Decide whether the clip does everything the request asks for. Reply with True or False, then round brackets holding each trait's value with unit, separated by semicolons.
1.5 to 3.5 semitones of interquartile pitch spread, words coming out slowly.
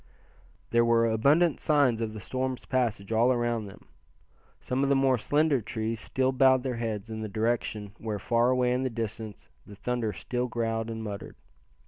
False (2.6 semitones; 180 wpm)